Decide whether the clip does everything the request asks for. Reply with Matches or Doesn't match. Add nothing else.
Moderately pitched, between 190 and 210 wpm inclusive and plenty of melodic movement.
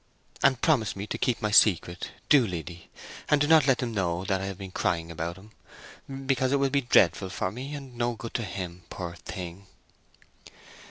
Doesn't match